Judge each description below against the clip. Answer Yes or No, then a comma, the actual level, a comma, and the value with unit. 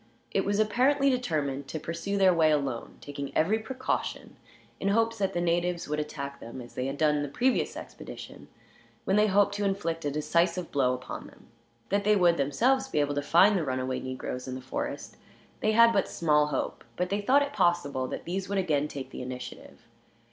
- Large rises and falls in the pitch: Yes, wide, 6.2 semitones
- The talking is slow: No, fast, 205 wpm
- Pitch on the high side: No, medium, 170 Hz